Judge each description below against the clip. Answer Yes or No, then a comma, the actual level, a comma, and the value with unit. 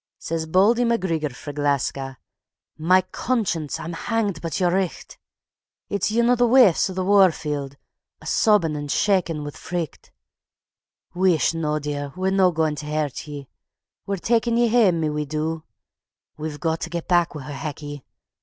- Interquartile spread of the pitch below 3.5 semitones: No, average, 4.4 semitones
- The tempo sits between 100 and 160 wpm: No, average, 170 wpm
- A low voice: No, medium, 165 Hz